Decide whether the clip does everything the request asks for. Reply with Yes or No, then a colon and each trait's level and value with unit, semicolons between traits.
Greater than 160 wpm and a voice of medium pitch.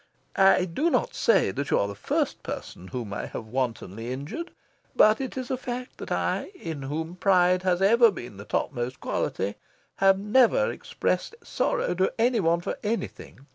Yes: average, 175 wpm; medium, 180 Hz